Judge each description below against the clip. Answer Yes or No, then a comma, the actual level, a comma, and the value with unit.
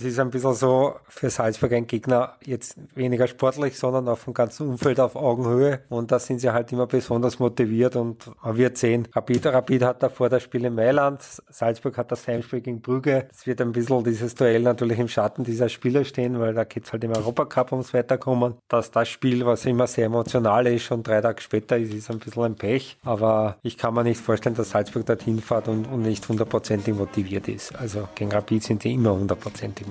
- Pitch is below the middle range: Yes, low, 120 Hz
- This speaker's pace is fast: Yes, fast, 215 wpm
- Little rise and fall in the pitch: Yes, narrow, 1.9 semitones